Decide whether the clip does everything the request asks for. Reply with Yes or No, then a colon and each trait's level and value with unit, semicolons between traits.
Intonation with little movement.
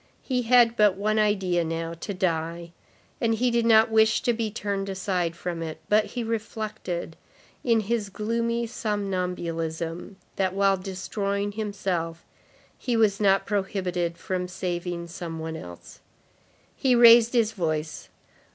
No: average, 4.3 semitones